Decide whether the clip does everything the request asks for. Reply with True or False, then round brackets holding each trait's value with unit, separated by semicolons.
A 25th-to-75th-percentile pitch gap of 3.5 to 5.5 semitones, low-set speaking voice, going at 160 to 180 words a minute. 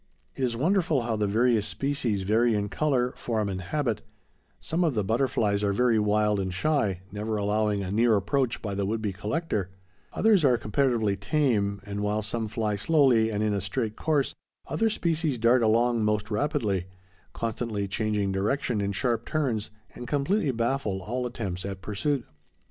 True (4.2 semitones; 110 Hz; 170 wpm)